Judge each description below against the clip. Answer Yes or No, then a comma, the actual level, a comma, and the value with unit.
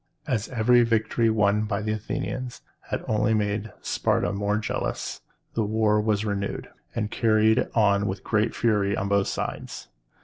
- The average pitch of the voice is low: Yes, low, 105 Hz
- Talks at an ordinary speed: Yes, average, 150 wpm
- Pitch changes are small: Yes, narrow, 1.5 semitones